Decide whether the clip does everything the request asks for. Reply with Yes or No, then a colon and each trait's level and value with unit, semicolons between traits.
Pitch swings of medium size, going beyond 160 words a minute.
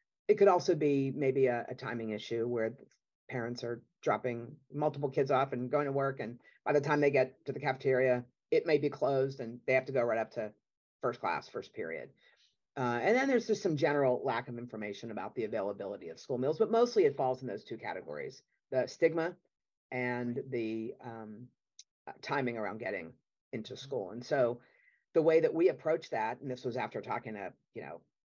Yes: average, 4.2 semitones; average, 200 wpm